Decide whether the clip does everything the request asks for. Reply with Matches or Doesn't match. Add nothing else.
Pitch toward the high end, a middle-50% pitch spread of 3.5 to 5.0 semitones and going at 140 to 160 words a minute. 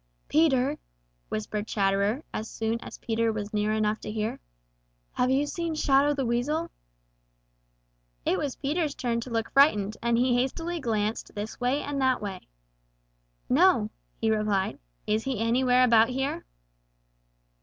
Matches